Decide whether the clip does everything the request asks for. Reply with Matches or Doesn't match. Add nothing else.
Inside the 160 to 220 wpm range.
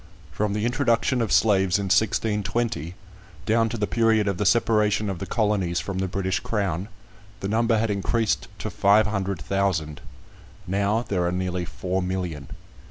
Matches